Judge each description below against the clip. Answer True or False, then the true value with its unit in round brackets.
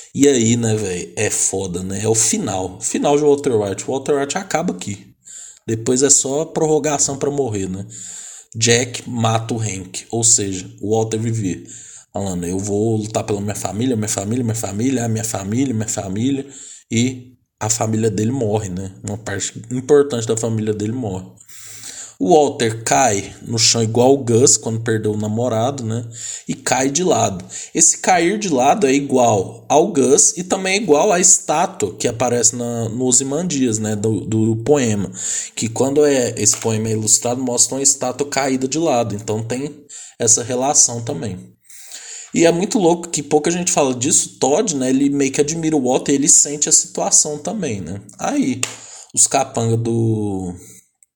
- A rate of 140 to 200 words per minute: True (180 wpm)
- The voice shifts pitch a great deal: False (4.4 semitones)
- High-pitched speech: False (120 Hz)